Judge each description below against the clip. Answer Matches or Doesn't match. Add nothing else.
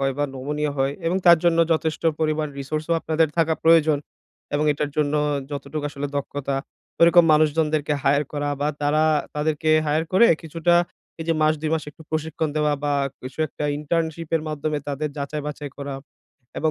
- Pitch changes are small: Matches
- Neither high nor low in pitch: Matches